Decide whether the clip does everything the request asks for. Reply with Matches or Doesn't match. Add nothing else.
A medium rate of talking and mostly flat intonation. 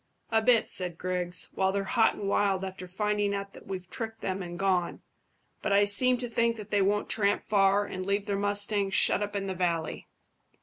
Doesn't match